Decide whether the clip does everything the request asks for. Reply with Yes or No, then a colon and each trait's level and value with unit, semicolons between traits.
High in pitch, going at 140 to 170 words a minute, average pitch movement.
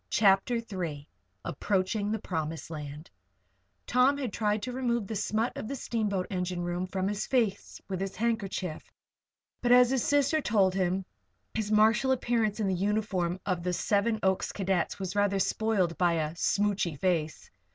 Yes: high, 200 Hz; average, 160 wpm; average, 3.5 semitones